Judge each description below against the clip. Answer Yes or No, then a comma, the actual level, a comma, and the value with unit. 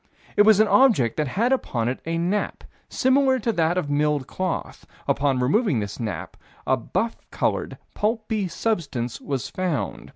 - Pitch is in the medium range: Yes, medium, 170 Hz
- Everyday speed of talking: Yes, average, 160 wpm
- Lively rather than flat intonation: Yes, wide, 8.5 semitones